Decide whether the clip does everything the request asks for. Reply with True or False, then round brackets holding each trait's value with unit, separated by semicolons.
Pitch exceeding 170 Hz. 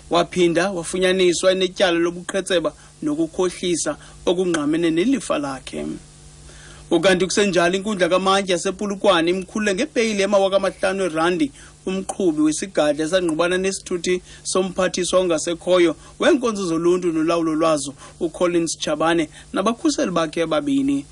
True (185 Hz)